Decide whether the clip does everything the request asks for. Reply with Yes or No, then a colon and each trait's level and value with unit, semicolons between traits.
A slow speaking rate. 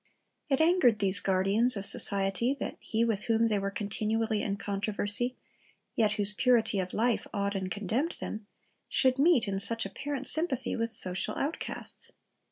No: average, 160 wpm